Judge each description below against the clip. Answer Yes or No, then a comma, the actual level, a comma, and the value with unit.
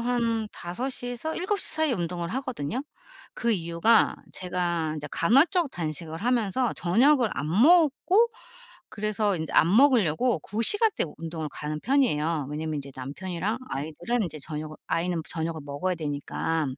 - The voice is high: No, medium, 180 Hz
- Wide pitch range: Yes, wide, 7.5 semitones